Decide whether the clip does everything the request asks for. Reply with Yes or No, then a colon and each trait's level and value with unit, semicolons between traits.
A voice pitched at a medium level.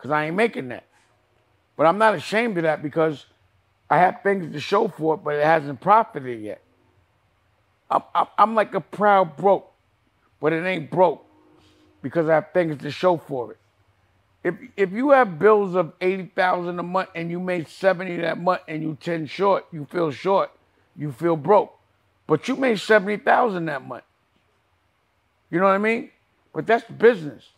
Yes: medium, 170 Hz